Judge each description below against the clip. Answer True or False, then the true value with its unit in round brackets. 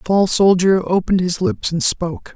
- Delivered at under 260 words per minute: True (205 wpm)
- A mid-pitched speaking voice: True (175 Hz)